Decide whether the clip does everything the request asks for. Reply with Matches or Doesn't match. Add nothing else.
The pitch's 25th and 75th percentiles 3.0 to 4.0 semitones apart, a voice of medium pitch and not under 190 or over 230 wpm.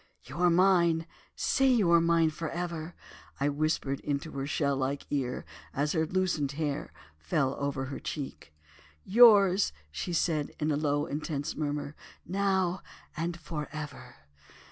Doesn't match